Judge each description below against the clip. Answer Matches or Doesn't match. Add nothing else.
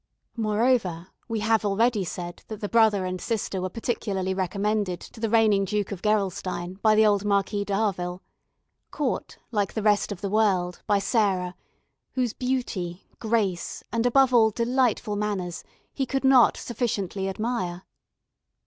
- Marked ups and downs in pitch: Doesn't match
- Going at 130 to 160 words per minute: Matches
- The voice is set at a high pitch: Matches